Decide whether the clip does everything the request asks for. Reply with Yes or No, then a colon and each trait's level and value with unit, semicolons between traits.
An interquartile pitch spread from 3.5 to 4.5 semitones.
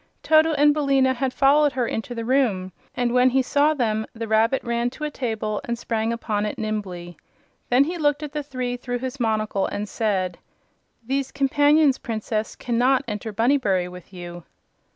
Yes: average, 4.2 semitones